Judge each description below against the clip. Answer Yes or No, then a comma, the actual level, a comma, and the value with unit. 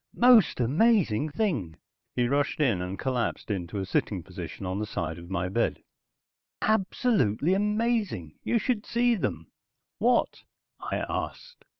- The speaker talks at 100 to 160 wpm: Yes, slow, 135 wpm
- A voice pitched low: Yes, low, 125 Hz